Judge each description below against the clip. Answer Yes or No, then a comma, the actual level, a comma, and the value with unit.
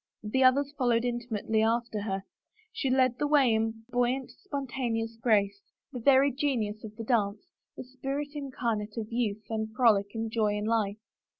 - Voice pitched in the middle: No, high, 230 Hz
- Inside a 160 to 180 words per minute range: Yes, average, 170 wpm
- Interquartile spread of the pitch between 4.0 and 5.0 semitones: No, average, 3.1 semitones